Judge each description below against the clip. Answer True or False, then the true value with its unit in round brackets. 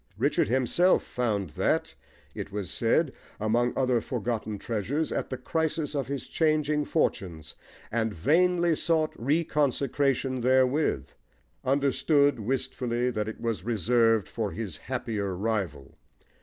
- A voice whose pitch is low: True (125 Hz)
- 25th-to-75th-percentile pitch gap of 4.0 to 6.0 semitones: True (4.7 semitones)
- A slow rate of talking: True (120 wpm)